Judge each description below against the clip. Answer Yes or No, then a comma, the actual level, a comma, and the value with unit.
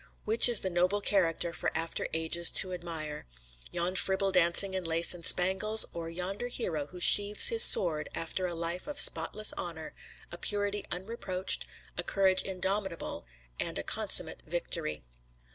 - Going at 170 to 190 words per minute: No, average, 155 wpm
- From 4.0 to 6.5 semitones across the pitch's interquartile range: No, average, 2.8 semitones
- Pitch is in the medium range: Yes, medium, 180 Hz